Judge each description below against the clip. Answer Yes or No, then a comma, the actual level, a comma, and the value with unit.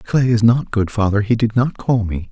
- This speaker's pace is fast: Yes, fast, 235 wpm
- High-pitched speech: No, low, 110 Hz